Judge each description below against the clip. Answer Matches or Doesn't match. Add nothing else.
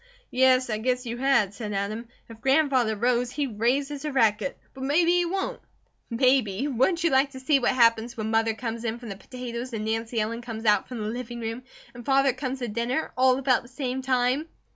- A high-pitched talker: Matches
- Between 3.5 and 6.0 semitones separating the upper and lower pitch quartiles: Doesn't match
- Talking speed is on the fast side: Matches